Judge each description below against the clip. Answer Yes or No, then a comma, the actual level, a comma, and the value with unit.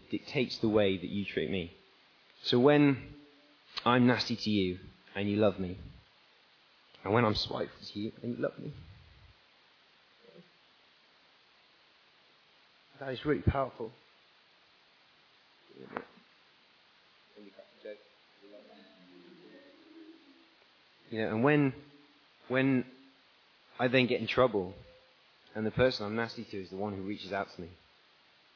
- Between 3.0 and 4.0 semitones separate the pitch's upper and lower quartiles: No, wide, 5.5 semitones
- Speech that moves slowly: Yes, slow, 120 wpm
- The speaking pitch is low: Yes, low, 120 Hz